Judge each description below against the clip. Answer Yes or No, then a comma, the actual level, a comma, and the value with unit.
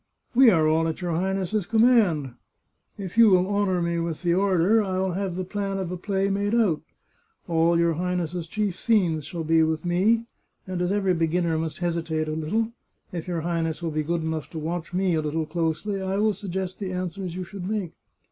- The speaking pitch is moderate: Yes, medium, 180 Hz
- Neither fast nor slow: No, fast, 215 wpm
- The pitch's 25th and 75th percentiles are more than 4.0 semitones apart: No, average, 3.1 semitones